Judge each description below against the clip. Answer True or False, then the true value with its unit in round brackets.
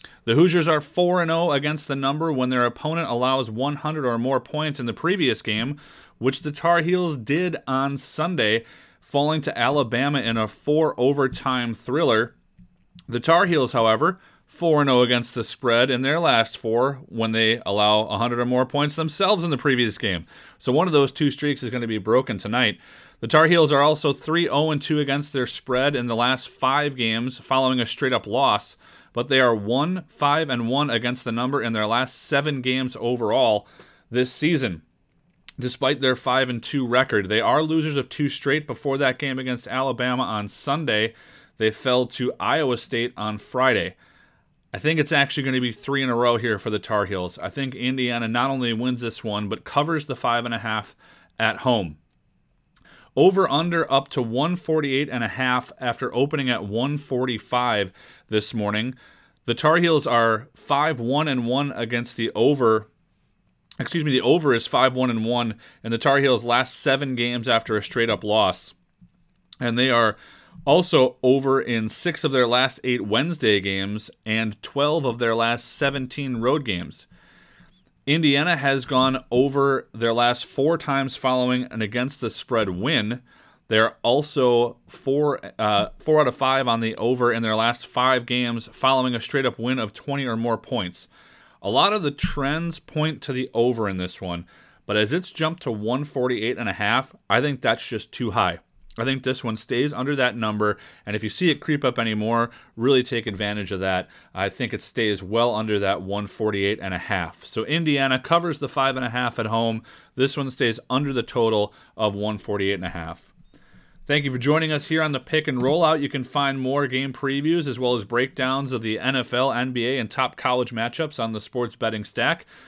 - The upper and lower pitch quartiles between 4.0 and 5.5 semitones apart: False (3.6 semitones)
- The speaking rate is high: False (185 wpm)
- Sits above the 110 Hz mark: True (125 Hz)